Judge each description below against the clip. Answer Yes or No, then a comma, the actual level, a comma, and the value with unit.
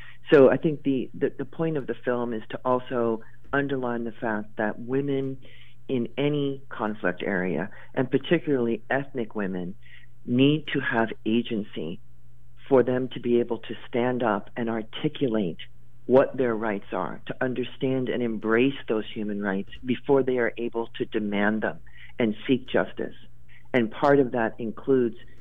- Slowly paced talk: No, average, 155 wpm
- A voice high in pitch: No, low, 120 Hz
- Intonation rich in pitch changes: No, average, 3.2 semitones